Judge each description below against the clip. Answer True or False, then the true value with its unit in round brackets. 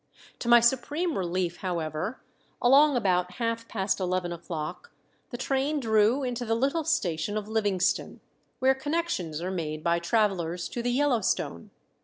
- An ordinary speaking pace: True (145 wpm)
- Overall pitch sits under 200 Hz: False (215 Hz)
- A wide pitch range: True (6.6 semitones)